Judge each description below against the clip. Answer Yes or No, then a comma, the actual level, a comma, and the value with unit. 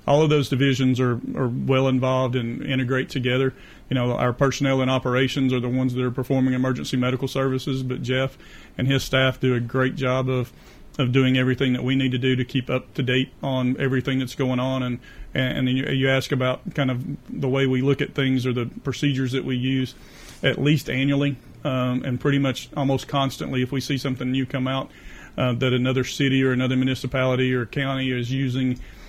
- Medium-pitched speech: No, low, 130 Hz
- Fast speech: Yes, fast, 210 wpm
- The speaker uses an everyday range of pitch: No, narrow, 0.9 semitones